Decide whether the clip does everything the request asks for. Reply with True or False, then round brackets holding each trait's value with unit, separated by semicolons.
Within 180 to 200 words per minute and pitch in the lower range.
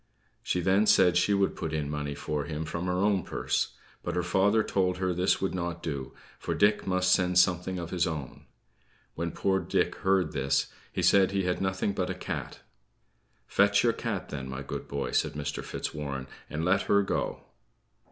True (190 wpm; 90 Hz)